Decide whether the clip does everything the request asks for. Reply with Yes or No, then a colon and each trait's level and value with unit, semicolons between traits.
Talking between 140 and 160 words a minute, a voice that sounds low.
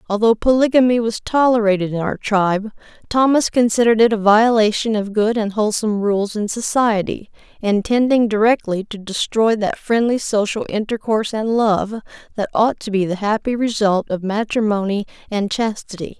No: average, 150 wpm; high, 215 Hz